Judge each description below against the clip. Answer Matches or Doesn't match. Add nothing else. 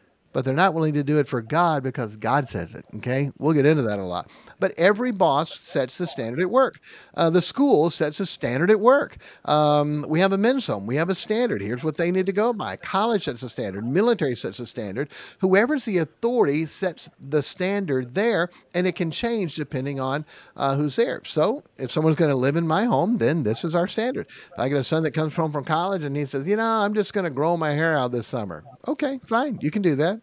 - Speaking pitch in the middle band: Matches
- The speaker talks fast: Matches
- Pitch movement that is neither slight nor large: Doesn't match